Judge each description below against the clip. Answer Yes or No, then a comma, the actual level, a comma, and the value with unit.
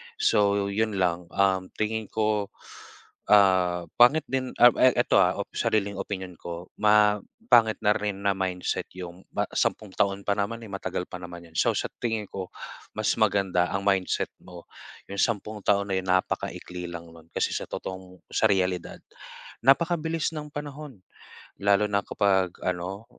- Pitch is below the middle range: Yes, low, 100 Hz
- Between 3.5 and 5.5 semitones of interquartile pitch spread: No, average, 2.8 semitones